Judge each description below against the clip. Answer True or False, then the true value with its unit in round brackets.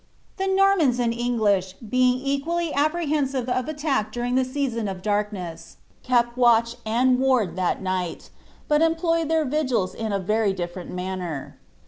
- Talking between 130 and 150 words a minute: True (145 wpm)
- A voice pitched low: False (245 Hz)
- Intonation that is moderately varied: False (6.0 semitones)